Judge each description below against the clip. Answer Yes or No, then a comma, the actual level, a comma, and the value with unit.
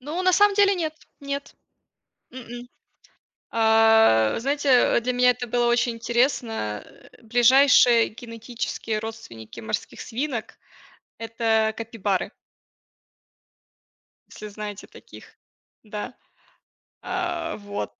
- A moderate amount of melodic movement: Yes, average, 3.1 semitones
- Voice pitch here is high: Yes, high, 235 Hz